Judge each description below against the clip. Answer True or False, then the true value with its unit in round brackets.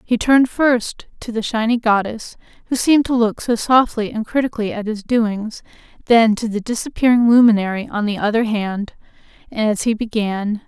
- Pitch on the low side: False (225 Hz)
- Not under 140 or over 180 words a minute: True (170 wpm)